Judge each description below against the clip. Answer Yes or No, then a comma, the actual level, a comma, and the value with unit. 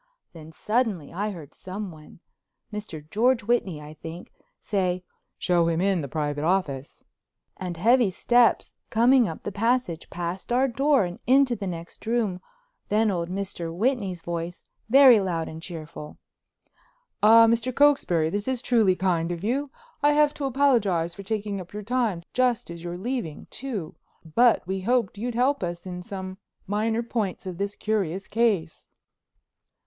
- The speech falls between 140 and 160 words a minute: Yes, average, 155 wpm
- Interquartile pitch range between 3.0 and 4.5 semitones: No, wide, 5.5 semitones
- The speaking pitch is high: Yes, high, 195 Hz